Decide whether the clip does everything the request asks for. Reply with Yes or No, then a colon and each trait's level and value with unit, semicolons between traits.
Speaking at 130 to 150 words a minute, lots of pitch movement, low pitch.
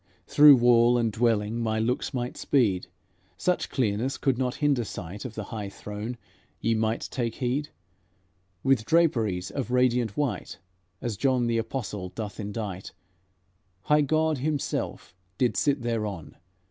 No: average, 140 wpm; average, 3.6 semitones; low, 120 Hz